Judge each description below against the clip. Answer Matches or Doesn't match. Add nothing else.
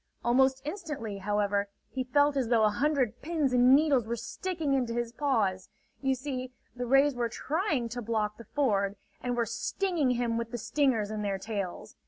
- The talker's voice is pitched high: Matches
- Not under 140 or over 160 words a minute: Doesn't match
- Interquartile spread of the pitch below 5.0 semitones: Matches